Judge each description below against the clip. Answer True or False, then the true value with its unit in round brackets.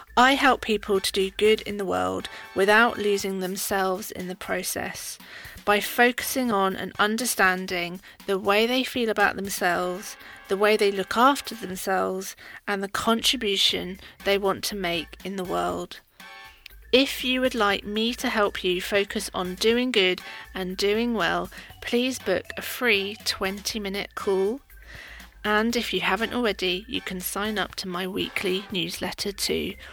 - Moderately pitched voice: False (200 Hz)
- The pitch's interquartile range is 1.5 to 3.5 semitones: True (3.1 semitones)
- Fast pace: False (155 wpm)